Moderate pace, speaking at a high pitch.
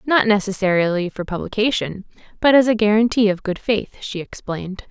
Yes: average, 160 wpm; high, 205 Hz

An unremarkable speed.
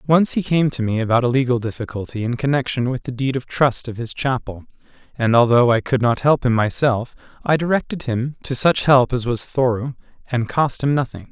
No: fast, 210 wpm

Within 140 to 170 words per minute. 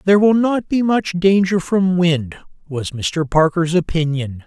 Yes: average, 160 wpm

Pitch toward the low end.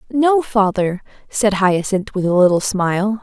No: high, 205 Hz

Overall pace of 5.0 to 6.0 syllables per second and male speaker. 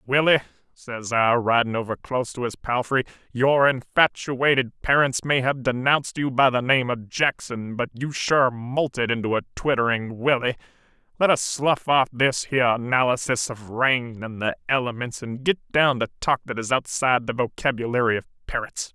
Yes: 5.1 syllables/s; male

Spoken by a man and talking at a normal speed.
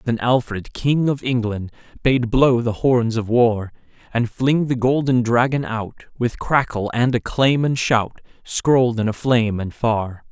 Yes: male; average, 165 wpm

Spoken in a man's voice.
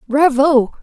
No: female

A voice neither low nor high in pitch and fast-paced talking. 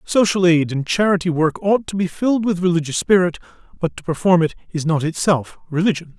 No: medium, 175 Hz; average, 195 wpm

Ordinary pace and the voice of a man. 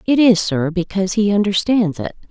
No: average, 180 wpm; female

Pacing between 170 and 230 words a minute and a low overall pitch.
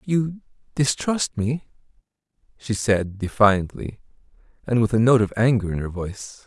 No: average, 140 wpm; low, 115 Hz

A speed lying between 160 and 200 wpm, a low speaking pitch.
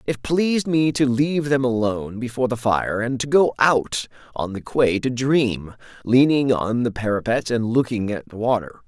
Yes: average, 190 wpm; low, 125 Hz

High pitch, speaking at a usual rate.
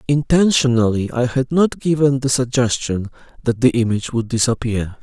No: low, 125 Hz; average, 145 wpm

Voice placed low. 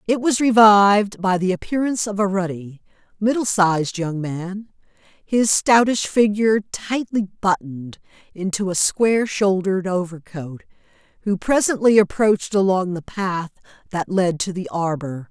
No: high, 195 Hz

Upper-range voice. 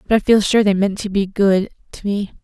Yes: high, 200 Hz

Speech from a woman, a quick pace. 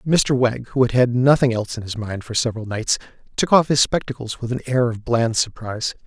No: male; fast, 230 wpm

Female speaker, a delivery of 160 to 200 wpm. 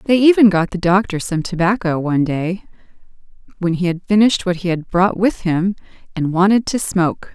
Yes: female; average, 190 wpm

